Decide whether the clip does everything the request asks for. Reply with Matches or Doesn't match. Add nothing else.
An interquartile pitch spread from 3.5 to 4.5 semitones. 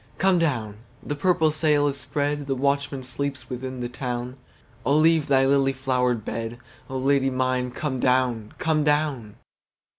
Doesn't match